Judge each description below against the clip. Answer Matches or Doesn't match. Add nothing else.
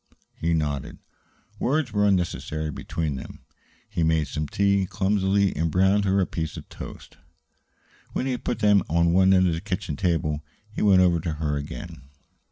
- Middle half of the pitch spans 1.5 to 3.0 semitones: Doesn't match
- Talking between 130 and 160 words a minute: Doesn't match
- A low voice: Matches